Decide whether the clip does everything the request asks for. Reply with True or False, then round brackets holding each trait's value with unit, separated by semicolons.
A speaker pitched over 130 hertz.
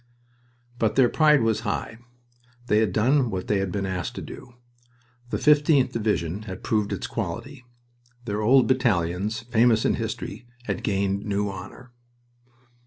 False (110 Hz)